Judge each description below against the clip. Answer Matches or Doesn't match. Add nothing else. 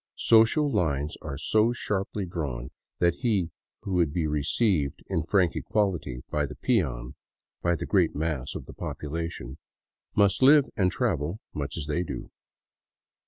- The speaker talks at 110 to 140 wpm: Doesn't match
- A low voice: Matches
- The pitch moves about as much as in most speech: Doesn't match